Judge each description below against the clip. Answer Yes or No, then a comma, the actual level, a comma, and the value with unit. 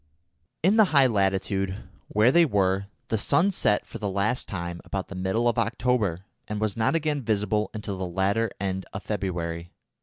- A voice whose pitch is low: Yes, low, 105 Hz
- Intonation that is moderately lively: Yes, average, 3.4 semitones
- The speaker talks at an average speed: Yes, average, 180 wpm